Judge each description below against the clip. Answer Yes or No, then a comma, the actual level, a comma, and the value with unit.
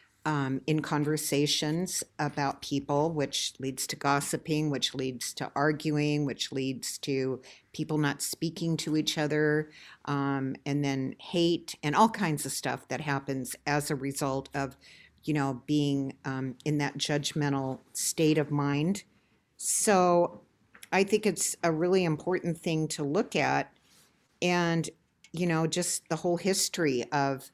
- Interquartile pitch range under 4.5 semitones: Yes, average, 2.9 semitones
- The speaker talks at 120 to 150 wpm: Yes, average, 145 wpm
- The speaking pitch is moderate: Yes, medium, 150 Hz